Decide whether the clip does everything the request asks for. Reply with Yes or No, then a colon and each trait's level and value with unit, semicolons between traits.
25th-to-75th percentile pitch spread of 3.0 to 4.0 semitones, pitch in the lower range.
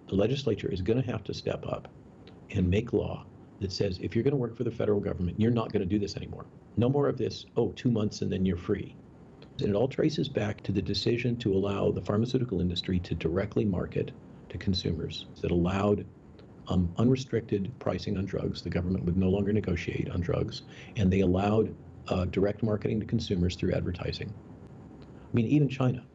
Yes: average, 3.7 semitones; low, 105 Hz